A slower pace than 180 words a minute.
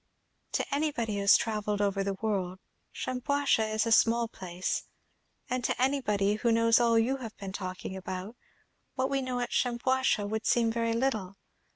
Yes: average, 170 wpm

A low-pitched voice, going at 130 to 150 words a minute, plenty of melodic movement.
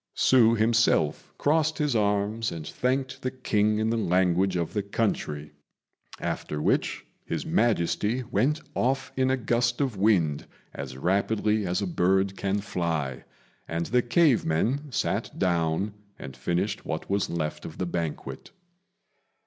Yes: low, 105 Hz; average, 145 wpm; wide, 5.8 semitones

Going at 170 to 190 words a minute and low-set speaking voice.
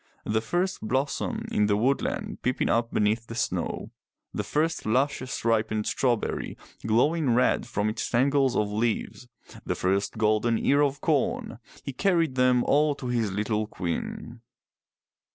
No: average, 150 wpm; low, 120 Hz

